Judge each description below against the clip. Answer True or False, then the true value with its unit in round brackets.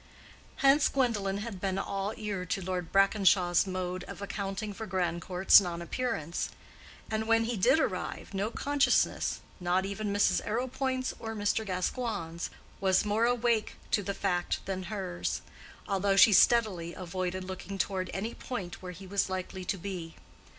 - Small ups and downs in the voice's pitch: False (3.0 semitones)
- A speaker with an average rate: True (145 wpm)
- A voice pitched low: False (195 Hz)